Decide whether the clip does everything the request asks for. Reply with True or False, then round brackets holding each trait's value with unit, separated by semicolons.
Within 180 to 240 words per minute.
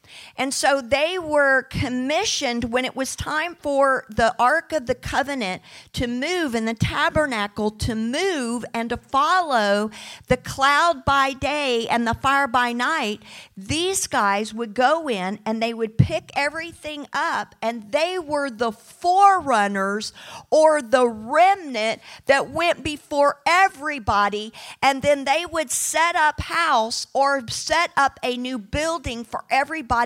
False (145 wpm)